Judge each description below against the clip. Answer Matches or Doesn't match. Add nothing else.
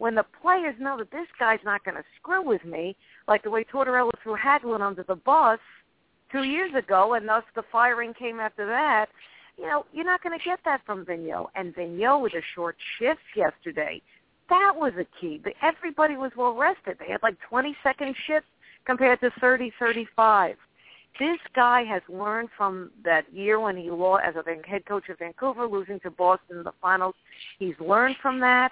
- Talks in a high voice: Matches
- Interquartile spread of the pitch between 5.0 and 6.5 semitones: Matches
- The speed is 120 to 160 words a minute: Doesn't match